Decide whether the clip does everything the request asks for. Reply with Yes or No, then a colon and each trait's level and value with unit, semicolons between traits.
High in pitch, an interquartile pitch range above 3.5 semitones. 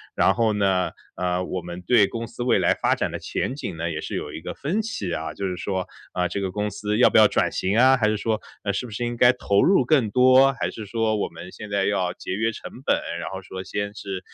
No: low, 105 Hz; average, 4.1 semitones